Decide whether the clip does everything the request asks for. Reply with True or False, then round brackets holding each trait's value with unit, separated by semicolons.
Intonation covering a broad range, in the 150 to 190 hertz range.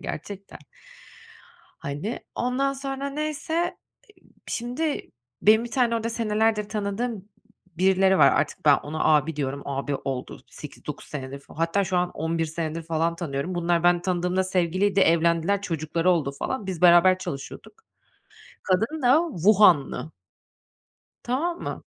True (5.7 semitones; 185 Hz)